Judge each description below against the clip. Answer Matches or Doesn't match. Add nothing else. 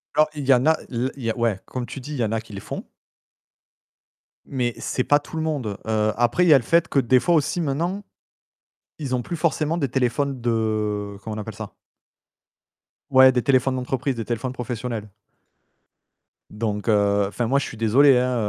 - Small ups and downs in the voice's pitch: Doesn't match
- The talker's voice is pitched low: Matches